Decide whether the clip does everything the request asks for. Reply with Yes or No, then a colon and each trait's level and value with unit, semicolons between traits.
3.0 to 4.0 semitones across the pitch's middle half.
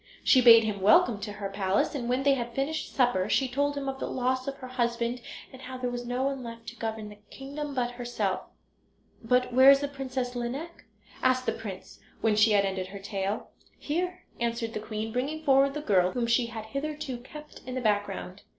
Yes: average, 3.7 semitones